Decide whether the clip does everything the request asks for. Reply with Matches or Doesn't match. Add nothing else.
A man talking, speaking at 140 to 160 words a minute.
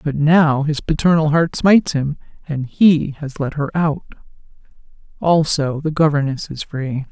Doesn't match